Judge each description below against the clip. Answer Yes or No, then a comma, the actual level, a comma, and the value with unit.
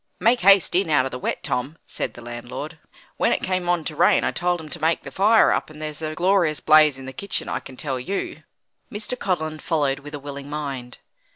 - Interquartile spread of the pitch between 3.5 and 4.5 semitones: Yes, average, 4.2 semitones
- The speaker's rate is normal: No, fast, 230 wpm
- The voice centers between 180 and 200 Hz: No, medium, 155 Hz